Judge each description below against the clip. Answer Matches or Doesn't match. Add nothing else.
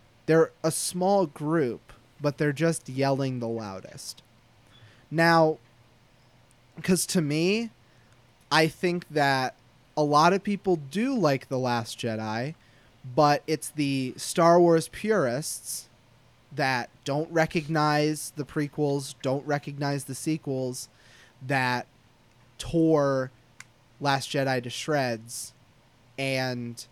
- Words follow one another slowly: Matches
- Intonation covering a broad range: Doesn't match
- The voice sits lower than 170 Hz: Matches